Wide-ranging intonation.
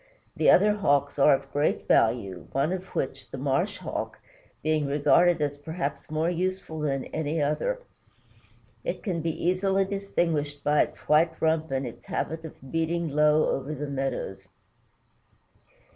No: average, 3.4 semitones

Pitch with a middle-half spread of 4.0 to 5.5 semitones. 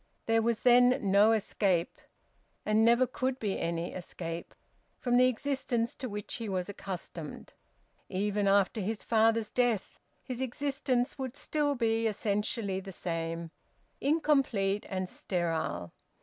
Yes: average, 4.6 semitones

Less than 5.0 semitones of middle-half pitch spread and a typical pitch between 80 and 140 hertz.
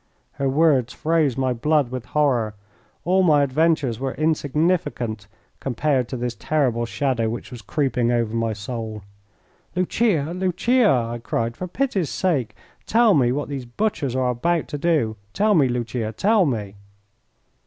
No: wide, 5.5 semitones; low, 135 Hz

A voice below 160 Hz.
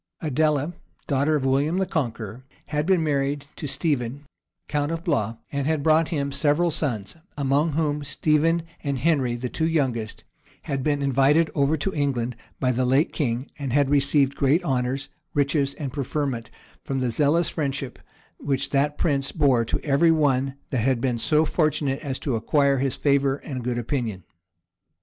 Yes: medium, 140 Hz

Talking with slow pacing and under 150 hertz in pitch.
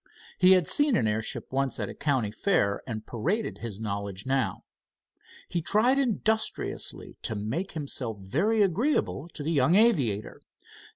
No: average, 150 wpm; medium, 140 Hz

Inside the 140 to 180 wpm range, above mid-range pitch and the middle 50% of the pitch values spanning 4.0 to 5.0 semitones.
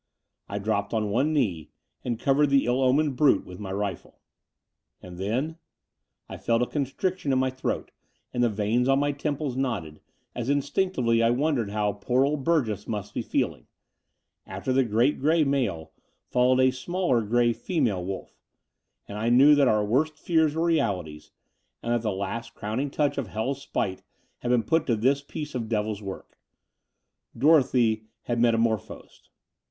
No: average, 165 wpm; low, 125 Hz; average, 4.7 semitones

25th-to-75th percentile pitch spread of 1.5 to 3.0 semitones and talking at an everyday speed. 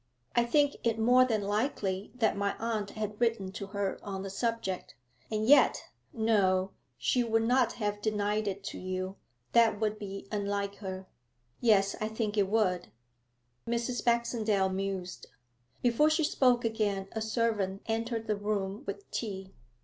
Yes: average, 2.7 semitones; average, 155 wpm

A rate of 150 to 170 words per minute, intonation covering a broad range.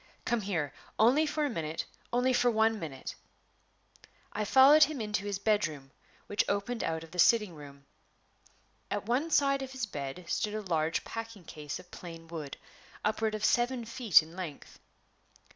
Yes: average, 165 wpm; wide, 6.6 semitones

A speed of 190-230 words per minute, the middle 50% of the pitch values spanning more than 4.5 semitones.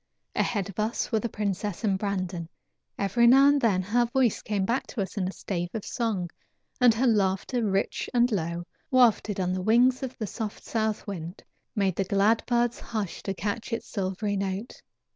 No: average, 195 wpm; average, 3.6 semitones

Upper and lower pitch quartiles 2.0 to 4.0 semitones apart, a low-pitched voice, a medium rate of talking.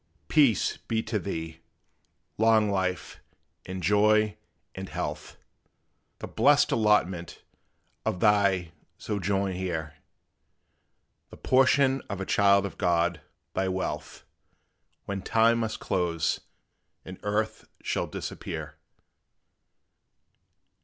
No: average, 3.0 semitones; low, 100 Hz; slow, 100 wpm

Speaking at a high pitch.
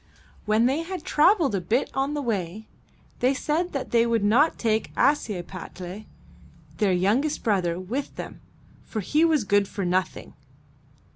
Yes: high, 225 Hz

